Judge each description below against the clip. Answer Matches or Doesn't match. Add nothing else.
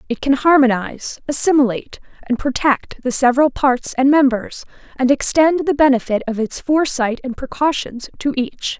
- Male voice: Doesn't match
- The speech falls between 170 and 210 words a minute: Doesn't match